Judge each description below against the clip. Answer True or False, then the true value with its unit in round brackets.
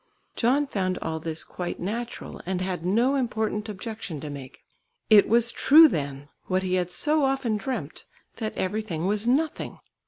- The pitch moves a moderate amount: True (5.0 semitones)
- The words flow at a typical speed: True (160 wpm)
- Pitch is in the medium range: False (210 Hz)